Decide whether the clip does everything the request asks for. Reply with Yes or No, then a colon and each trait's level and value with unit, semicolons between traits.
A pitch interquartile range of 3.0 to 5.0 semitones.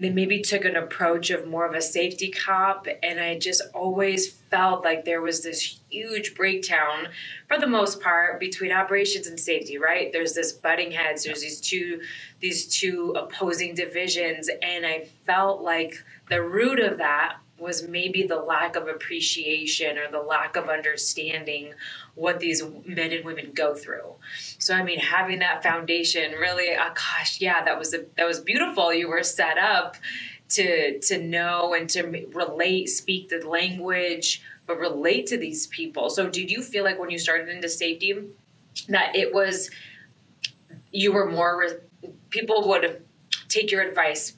No: narrow, 2.5 semitones